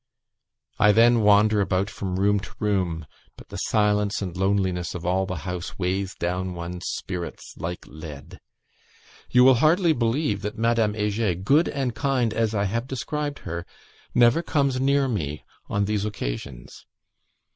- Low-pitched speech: Yes, low, 105 Hz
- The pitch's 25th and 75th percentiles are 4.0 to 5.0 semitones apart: Yes, average, 4.5 semitones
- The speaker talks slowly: No, average, 155 wpm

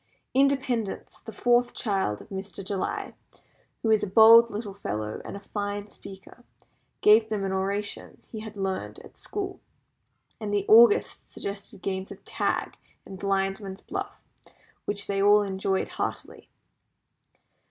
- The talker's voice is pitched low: No, high, 205 Hz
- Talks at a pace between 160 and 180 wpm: No, average, 140 wpm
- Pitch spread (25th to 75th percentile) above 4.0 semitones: No, narrow, 2.4 semitones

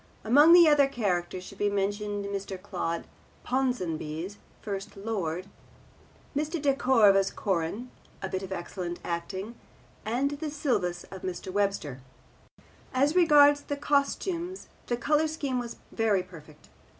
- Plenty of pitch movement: Yes, wide, 7.2 semitones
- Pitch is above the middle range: Yes, high, 205 Hz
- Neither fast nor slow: No, slow, 130 wpm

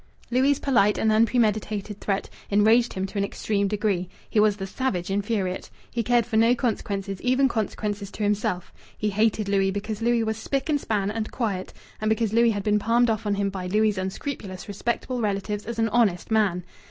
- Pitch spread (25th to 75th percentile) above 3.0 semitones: No, narrow, 2.5 semitones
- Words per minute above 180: Yes, average, 190 wpm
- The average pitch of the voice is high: Yes, high, 210 Hz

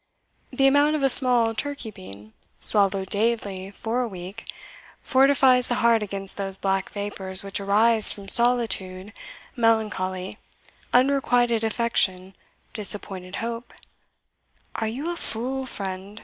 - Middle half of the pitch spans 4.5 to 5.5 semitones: No, average, 3.9 semitones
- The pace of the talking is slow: Yes, slow, 125 wpm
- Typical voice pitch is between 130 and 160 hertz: No, high, 220 Hz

